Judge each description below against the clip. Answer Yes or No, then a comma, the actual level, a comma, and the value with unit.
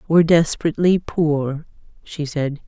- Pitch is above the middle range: No, medium, 155 Hz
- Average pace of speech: No, slow, 110 wpm